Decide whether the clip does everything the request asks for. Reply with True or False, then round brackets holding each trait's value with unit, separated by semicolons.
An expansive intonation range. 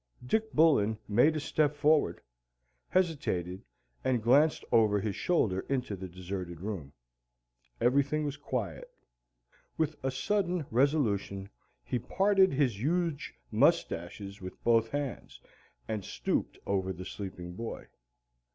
True (7.4 semitones)